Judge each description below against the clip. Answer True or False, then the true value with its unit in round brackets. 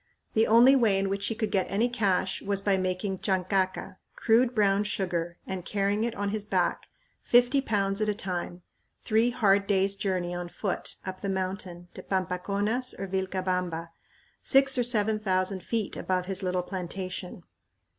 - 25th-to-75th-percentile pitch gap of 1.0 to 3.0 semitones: True (2.5 semitones)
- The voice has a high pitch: True (195 Hz)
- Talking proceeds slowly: False (165 wpm)